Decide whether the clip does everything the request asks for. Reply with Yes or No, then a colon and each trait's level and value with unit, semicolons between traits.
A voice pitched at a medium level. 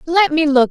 No: very high, 310 Hz